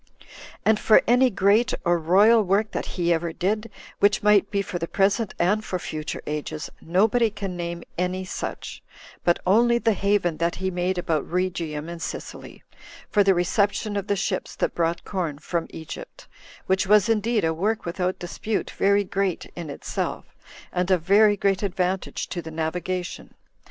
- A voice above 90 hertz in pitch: Yes, medium, 185 Hz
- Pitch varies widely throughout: No, average, 3.2 semitones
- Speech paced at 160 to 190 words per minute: Yes, average, 170 wpm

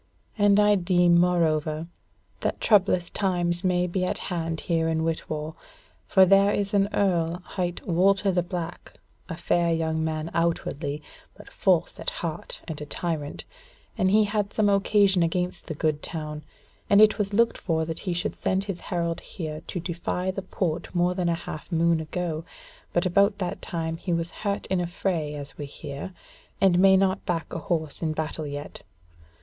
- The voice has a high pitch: No, medium, 175 Hz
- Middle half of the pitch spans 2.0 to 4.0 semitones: Yes, average, 2.9 semitones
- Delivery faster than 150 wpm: Yes, average, 180 wpm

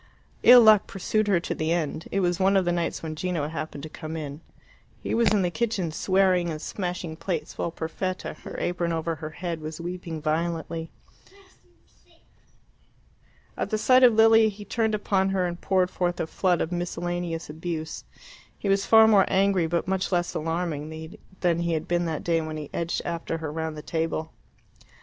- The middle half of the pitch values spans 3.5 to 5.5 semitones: No, average, 2.9 semitones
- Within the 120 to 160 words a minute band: No, average, 185 wpm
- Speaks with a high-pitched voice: No, medium, 175 Hz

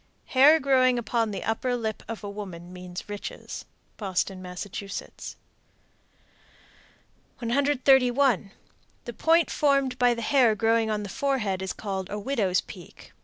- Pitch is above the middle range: Yes, high, 225 Hz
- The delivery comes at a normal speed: No, slow, 130 wpm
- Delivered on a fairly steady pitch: No, average, 4.6 semitones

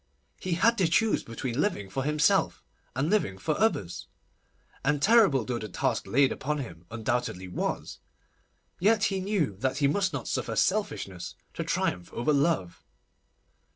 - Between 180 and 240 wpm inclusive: No, average, 155 wpm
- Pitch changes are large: Yes, wide, 8.8 semitones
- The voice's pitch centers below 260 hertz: Yes, medium, 140 Hz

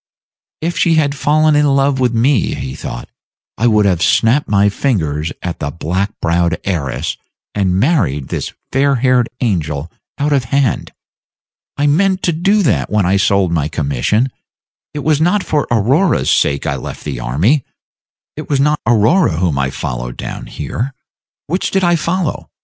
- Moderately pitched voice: No, low, 120 Hz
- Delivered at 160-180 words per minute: Yes, average, 165 wpm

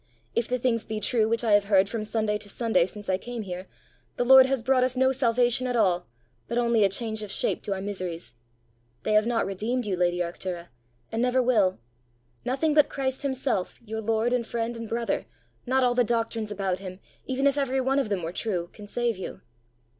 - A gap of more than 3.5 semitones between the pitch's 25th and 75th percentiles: Yes, average, 4.1 semitones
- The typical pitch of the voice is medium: No, high, 225 Hz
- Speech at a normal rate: No, fast, 215 wpm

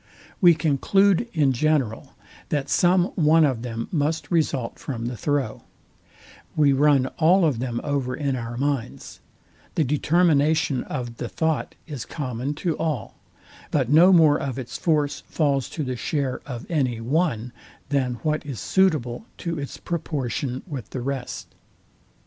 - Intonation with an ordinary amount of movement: Yes, average, 3.9 semitones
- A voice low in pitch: No, medium, 145 Hz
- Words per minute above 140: Yes, average, 150 wpm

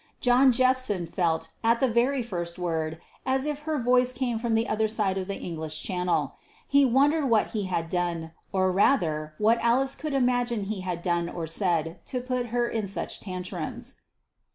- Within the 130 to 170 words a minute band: No, average, 180 wpm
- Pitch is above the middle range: Yes, high, 215 Hz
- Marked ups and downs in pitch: Yes, wide, 6.1 semitones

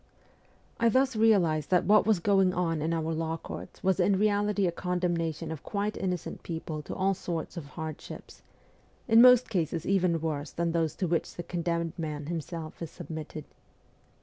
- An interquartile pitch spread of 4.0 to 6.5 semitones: No, average, 3.3 semitones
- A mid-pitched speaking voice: Yes, medium, 170 Hz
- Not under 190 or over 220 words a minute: No, average, 180 wpm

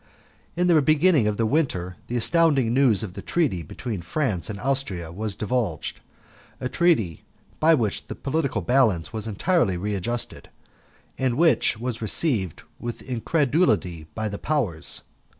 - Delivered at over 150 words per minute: No, average, 145 wpm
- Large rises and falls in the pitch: Yes, wide, 6.4 semitones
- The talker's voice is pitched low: Yes, low, 115 Hz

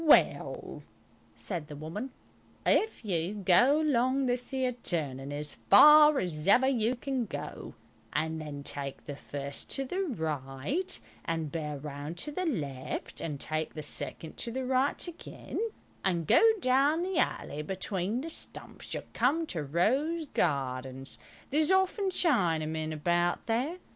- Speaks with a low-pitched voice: No, high, 190 Hz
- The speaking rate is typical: Yes, average, 145 wpm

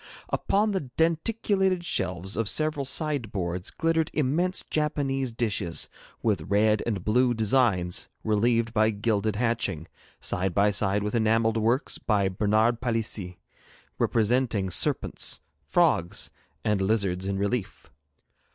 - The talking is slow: Yes, slow, 115 wpm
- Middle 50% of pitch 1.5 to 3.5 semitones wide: No, average, 4.7 semitones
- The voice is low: Yes, low, 110 Hz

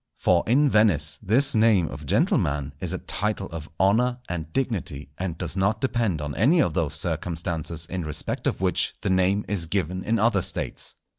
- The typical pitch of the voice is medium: No, very low, 95 Hz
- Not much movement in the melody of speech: No, average, 5.2 semitones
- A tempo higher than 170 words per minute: Yes, average, 180 wpm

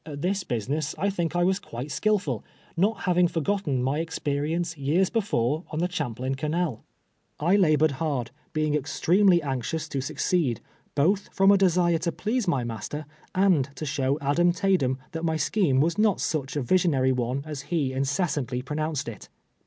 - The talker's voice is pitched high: No, medium, 155 Hz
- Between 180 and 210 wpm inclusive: No, average, 170 wpm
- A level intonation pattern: No, average, 4.6 semitones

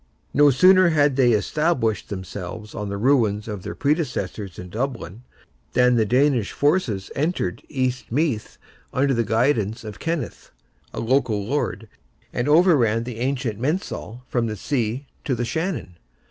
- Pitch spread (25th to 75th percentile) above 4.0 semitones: Yes, average, 5.1 semitones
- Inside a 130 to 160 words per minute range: Yes, average, 145 wpm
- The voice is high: No, low, 125 Hz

